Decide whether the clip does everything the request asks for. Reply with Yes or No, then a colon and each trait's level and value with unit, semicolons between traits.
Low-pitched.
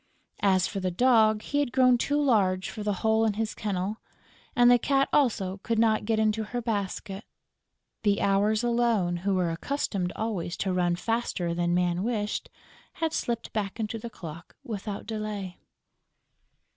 No: high, 215 Hz